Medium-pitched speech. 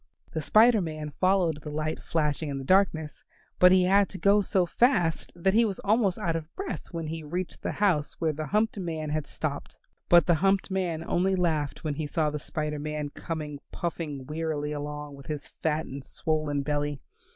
Yes: medium, 160 Hz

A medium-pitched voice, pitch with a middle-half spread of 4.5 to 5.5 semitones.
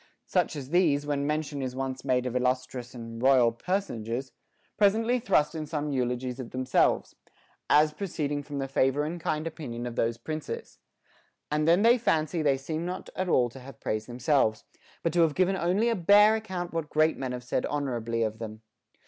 Yes: medium, 145 Hz; average, 4.9 semitones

